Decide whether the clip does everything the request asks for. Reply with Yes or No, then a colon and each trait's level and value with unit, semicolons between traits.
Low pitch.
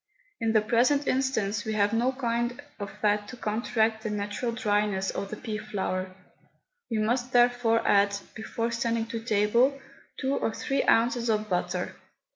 No: high, 225 Hz